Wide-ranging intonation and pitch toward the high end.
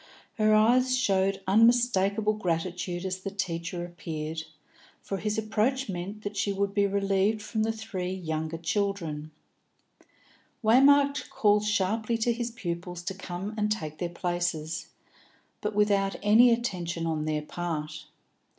No: average, 3.7 semitones; high, 195 Hz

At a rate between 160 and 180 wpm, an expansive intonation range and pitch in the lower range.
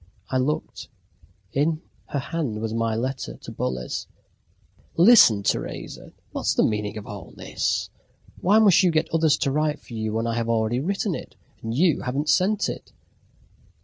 Yes: average, 175 wpm; wide, 6.5 semitones; low, 130 Hz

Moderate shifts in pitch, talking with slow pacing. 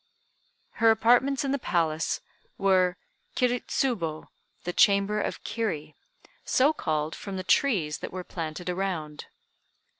No: wide, 6.1 semitones; slow, 125 wpm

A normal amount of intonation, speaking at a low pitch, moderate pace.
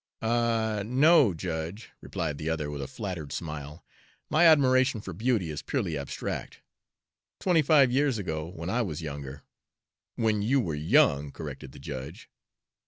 No: wide, 8.4 semitones; very low, 95 Hz; average, 150 wpm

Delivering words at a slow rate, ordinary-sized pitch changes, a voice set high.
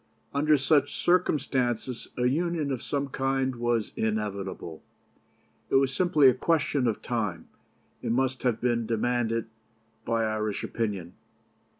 No: slow, 125 wpm; average, 3.6 semitones; low, 125 Hz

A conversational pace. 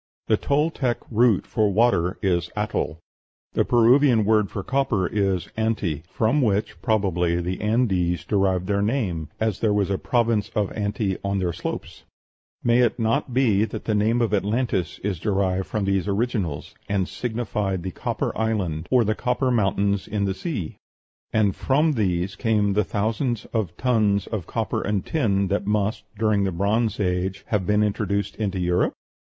Yes: average, 165 wpm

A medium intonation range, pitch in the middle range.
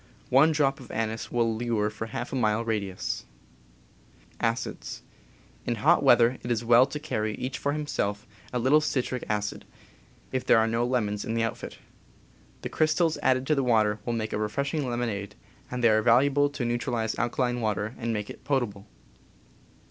No: average, 3.1 semitones; low, 120 Hz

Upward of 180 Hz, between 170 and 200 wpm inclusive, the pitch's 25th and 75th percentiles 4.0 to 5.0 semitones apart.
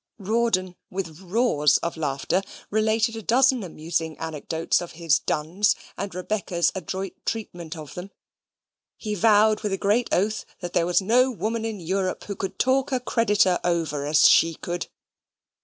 No: high, 190 Hz; average, 155 wpm; average, 4.5 semitones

